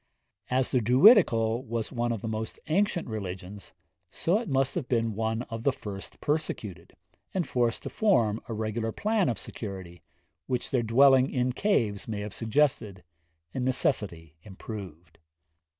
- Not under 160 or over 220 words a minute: No, average, 150 wpm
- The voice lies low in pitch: Yes, low, 115 Hz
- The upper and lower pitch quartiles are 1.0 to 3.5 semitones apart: No, average, 4.2 semitones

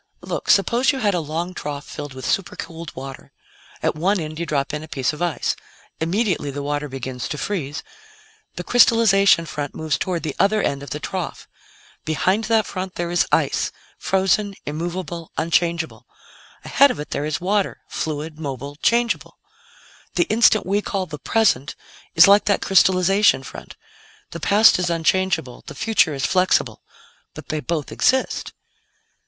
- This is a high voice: No, medium, 170 Hz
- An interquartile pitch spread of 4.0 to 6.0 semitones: Yes, average, 4.8 semitones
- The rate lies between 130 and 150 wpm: No, average, 160 wpm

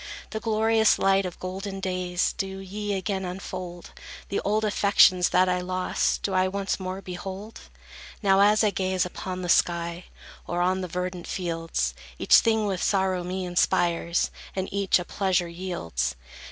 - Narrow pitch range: Yes, narrow, 1.7 semitones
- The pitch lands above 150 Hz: Yes, medium, 185 Hz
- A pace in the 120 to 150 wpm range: No, average, 160 wpm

